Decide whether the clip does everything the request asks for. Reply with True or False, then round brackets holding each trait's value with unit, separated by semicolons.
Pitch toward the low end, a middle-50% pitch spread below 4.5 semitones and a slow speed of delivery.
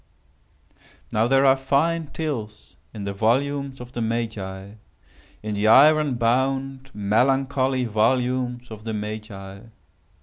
True (120 Hz; 3.9 semitones; 110 wpm)